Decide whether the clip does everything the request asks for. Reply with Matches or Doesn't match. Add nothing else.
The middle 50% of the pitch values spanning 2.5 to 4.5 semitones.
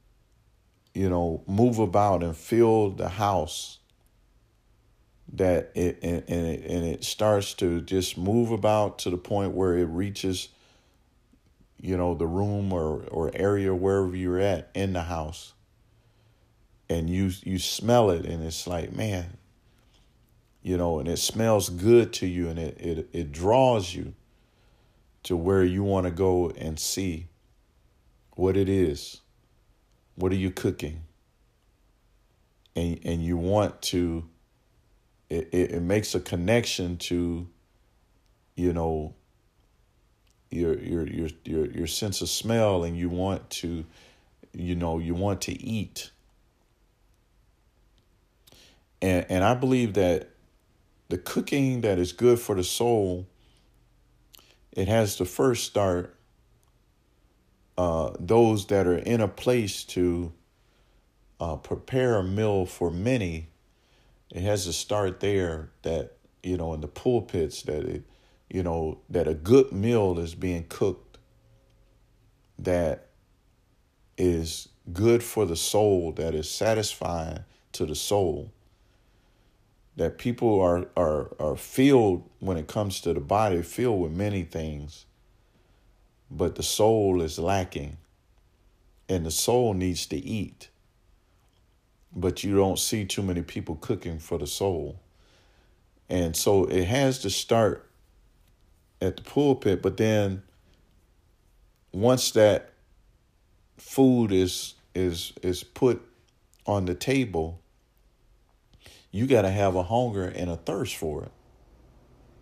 Matches